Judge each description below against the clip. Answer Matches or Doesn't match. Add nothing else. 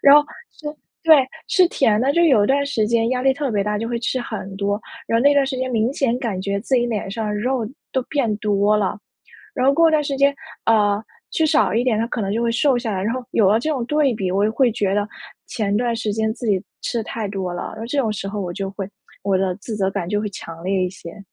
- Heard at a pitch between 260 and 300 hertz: Doesn't match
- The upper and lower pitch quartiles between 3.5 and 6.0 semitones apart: Matches